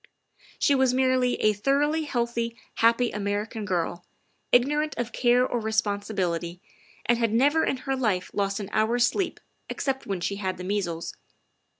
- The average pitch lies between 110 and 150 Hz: No, high, 230 Hz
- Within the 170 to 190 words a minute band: No, average, 155 wpm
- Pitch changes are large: No, average, 4.2 semitones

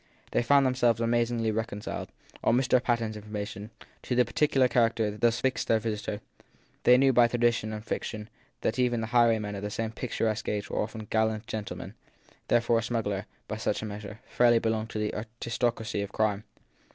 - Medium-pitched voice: No, low, 115 Hz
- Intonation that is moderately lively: No, narrow, 1.9 semitones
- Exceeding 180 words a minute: Yes, average, 190 wpm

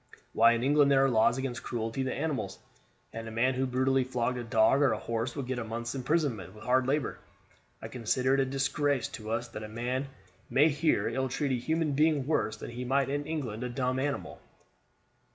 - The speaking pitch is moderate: No, low, 130 Hz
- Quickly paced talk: Yes, fast, 215 wpm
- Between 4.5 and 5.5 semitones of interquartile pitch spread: No, average, 2.9 semitones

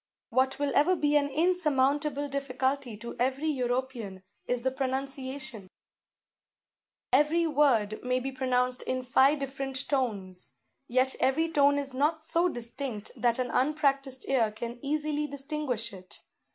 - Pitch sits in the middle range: No, very high, 265 Hz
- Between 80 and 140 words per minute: Yes, slow, 135 wpm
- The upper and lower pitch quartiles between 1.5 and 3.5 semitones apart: Yes, narrow, 2.5 semitones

